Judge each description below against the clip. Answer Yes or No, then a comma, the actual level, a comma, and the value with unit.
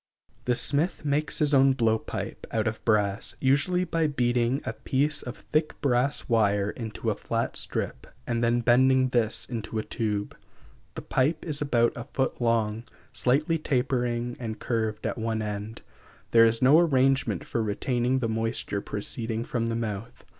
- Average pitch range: Yes, average, 3.1 semitones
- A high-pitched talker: No, low, 120 Hz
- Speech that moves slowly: No, average, 165 wpm